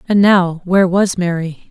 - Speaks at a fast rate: No, average, 175 wpm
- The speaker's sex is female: Yes, female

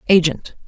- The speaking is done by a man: No, female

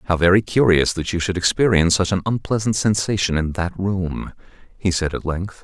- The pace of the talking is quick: No, average, 190 wpm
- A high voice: No, very low, 95 Hz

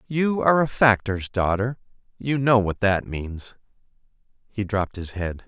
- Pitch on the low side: Yes, low, 110 Hz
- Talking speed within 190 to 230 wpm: No, average, 155 wpm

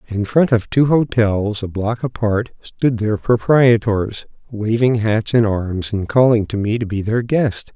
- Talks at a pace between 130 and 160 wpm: No, average, 180 wpm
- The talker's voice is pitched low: Yes, low, 110 Hz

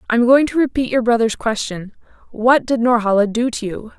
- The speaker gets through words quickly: No, average, 180 wpm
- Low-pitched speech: No, high, 235 Hz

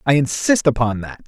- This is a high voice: No, low, 135 Hz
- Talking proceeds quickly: No, average, 190 wpm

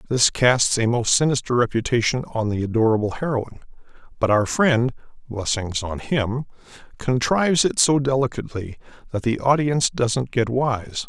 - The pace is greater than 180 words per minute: No, average, 140 wpm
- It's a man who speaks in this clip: Yes, male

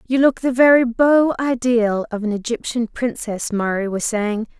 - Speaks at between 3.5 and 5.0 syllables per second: Yes, 4.4 syllables/s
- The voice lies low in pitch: No, high, 235 Hz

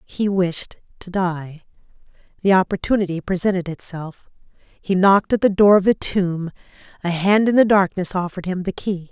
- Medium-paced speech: Yes, average, 165 wpm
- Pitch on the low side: No, medium, 185 Hz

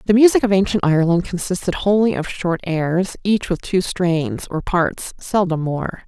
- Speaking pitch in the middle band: Yes, medium, 180 Hz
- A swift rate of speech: No, average, 170 wpm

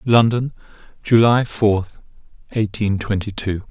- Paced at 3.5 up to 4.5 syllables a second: Yes, 3.9 syllables/s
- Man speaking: Yes, male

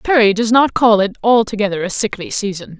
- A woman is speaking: Yes, female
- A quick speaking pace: No, average, 195 wpm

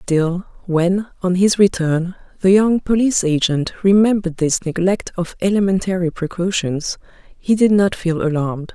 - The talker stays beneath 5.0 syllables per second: Yes, 4.7 syllables/s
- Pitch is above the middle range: No, medium, 180 Hz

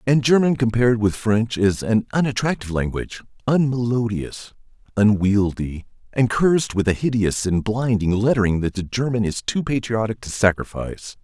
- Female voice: No, male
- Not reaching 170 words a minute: Yes, average, 145 wpm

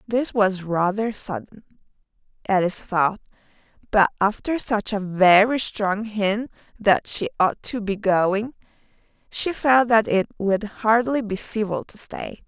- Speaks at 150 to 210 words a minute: No, average, 140 wpm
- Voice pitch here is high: Yes, high, 210 Hz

